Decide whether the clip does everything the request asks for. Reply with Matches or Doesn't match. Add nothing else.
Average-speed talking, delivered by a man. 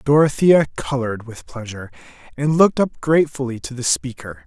Matches